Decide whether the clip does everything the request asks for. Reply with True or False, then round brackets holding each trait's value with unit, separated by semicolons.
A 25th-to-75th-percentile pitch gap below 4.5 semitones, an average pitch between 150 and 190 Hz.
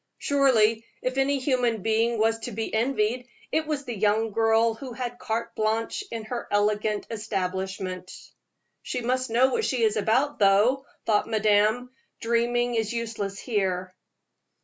False (2.7 semitones; 225 Hz)